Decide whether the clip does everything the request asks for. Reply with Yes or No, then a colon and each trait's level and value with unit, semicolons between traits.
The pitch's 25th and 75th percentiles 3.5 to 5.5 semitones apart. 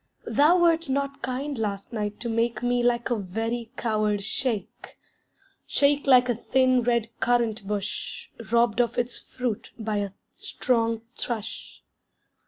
No: narrow, 2.6 semitones